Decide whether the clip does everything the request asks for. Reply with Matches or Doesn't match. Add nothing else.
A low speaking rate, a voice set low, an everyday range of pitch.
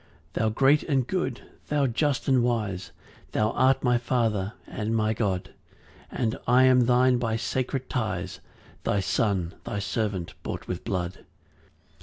Doesn't match